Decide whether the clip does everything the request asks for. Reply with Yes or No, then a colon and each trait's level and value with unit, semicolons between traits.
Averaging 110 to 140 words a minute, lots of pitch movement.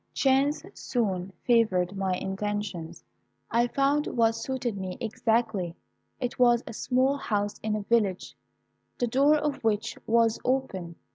No: slow, 135 wpm; average, 4.3 semitones